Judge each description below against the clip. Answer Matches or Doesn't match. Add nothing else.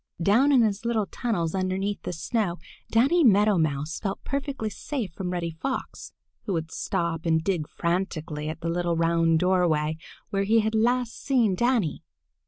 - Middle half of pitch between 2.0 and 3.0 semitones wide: Doesn't match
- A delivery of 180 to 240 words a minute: Doesn't match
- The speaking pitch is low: Doesn't match